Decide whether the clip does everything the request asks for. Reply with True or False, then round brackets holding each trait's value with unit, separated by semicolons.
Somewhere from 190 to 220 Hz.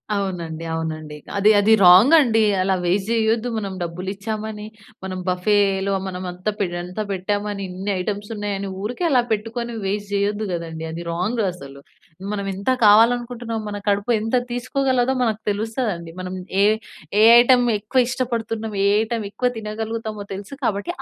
True (205 Hz)